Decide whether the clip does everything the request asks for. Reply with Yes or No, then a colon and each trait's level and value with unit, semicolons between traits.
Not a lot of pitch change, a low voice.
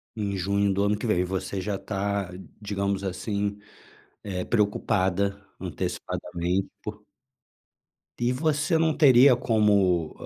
Yes: narrow, 2.2 semitones; low, 100 Hz